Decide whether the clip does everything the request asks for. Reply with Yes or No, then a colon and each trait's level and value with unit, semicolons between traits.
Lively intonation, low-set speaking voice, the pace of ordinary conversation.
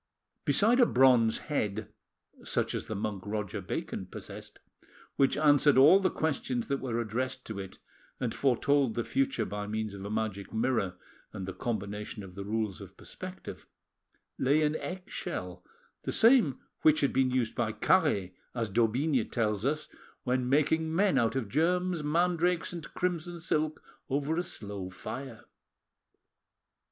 Yes: wide, 6.3 semitones; low, 130 Hz; average, 150 wpm